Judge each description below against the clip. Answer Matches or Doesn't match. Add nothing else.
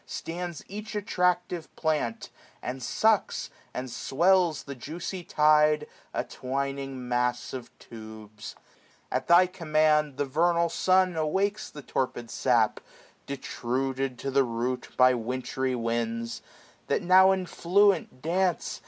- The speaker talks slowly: Matches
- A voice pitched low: Doesn't match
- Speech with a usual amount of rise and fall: Doesn't match